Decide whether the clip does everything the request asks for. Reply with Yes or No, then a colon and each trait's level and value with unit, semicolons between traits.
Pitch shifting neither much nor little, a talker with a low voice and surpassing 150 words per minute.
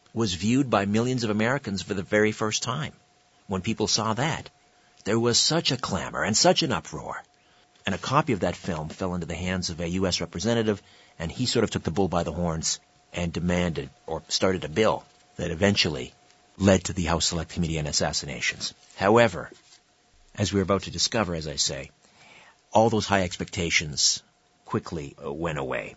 Yes: average, 4.4 semitones; low, 100 Hz; average, 185 wpm